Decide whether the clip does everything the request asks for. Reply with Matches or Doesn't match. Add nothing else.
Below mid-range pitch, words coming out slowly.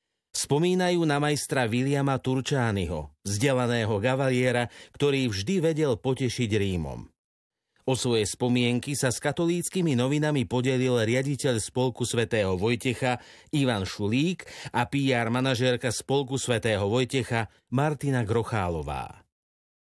Matches